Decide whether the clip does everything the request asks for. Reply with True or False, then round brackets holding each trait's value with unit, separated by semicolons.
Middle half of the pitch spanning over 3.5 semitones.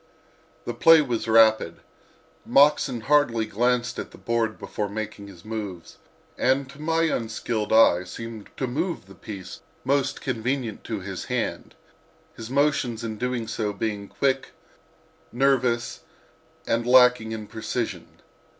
False (3.2 semitones)